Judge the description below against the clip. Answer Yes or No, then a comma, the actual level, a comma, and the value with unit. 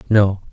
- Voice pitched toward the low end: Yes, low, 100 Hz